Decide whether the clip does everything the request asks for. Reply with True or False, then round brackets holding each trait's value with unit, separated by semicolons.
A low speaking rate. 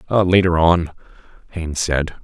True (105 wpm)